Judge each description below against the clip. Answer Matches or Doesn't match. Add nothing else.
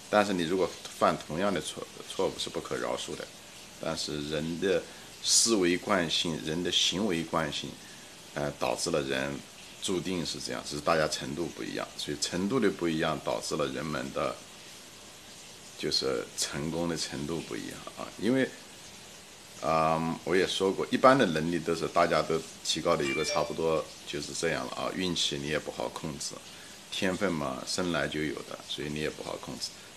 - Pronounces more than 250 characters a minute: Matches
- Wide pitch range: Doesn't match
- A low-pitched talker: Matches